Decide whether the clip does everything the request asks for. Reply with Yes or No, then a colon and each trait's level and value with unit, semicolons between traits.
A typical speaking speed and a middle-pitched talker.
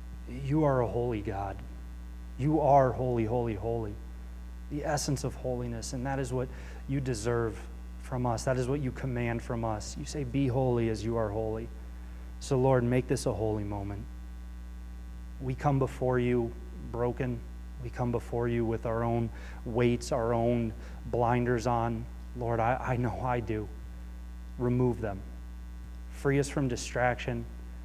No: average, 155 wpm; low, 115 Hz